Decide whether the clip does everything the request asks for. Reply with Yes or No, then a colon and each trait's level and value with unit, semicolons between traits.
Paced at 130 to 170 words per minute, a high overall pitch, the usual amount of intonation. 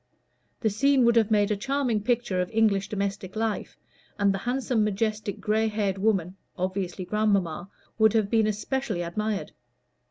No: average, 155 wpm; high, 210 Hz; narrow, 2.3 semitones